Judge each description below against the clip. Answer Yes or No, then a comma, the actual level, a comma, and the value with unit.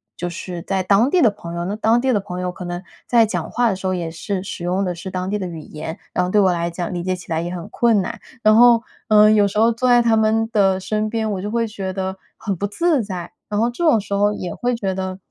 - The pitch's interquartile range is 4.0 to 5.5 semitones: No, average, 3.5 semitones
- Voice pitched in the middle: No, high, 195 Hz